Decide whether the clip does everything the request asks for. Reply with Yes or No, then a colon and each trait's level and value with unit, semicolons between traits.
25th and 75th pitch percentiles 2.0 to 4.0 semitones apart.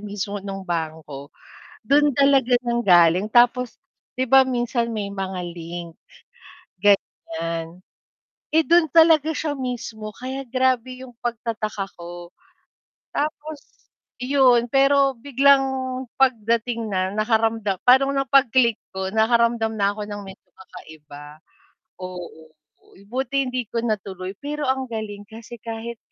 No: average, 5.1 semitones